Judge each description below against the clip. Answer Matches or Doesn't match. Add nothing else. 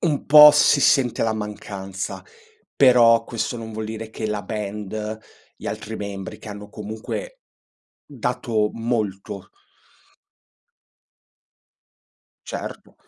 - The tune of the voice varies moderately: Doesn't match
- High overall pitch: Doesn't match